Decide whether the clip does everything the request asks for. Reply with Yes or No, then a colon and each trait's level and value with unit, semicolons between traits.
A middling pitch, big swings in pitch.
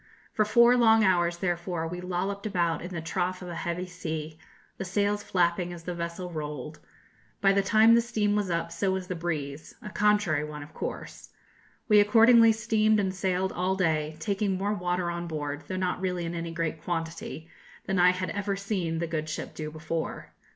No: medium, 180 Hz; average, 3.2 semitones